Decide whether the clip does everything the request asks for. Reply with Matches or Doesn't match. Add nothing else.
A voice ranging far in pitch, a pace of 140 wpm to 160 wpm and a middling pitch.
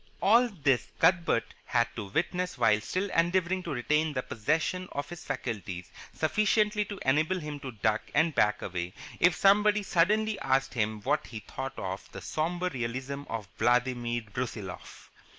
Matches